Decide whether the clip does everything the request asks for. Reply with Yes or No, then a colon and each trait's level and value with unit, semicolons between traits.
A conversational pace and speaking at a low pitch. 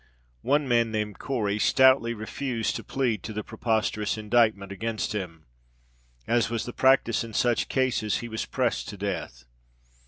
Yes: average, 155 wpm; low, 115 Hz